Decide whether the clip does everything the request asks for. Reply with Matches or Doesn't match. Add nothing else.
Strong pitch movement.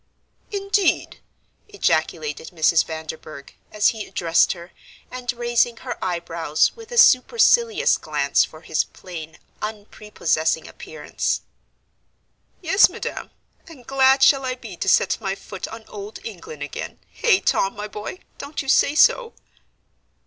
Matches